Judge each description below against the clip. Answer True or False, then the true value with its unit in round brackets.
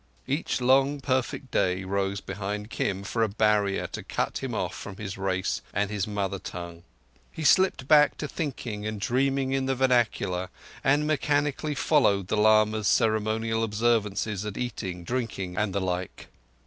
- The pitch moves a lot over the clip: False (5.0 semitones)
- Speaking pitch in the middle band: False (110 Hz)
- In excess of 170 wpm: False (160 wpm)